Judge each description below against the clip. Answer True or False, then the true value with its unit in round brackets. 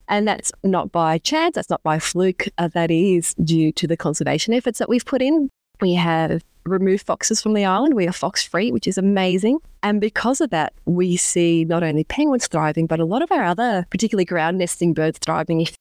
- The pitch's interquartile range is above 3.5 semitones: True (4.8 semitones)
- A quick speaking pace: True (215 wpm)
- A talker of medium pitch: True (180 Hz)